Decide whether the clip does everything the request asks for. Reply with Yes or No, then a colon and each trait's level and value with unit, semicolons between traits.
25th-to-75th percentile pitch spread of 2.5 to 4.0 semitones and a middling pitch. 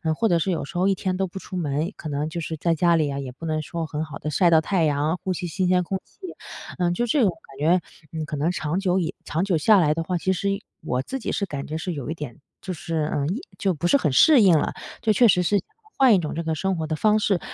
Yes: average, 3.6 semitones; medium, 170 Hz